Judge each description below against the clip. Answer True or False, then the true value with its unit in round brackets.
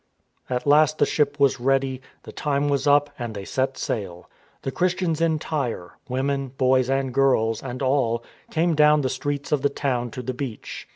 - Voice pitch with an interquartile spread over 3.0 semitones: False (2.5 semitones)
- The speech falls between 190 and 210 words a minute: True (195 wpm)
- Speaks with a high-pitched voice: False (135 Hz)